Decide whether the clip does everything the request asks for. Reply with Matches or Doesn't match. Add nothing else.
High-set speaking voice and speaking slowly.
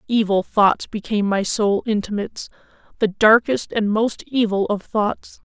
Matches